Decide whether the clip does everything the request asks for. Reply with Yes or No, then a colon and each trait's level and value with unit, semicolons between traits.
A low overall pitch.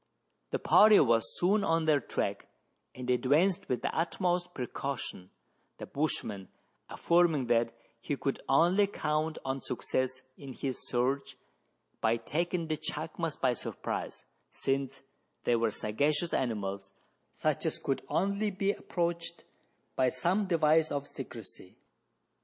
No: medium, 145 Hz